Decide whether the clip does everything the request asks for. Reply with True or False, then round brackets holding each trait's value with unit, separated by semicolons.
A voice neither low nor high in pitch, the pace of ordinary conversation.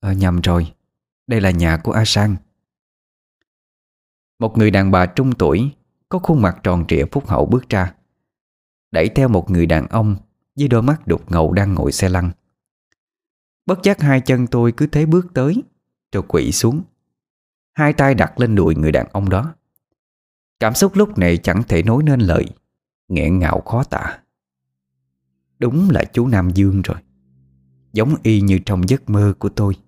False (100 Hz; 175 wpm)